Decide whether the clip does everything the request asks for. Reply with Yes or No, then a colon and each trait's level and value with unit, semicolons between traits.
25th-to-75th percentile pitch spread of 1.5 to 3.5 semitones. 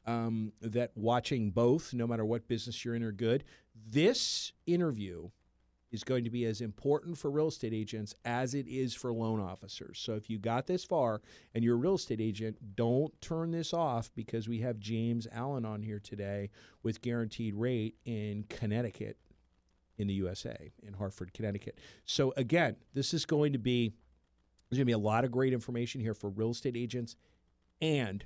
Yes: average, 2.9 semitones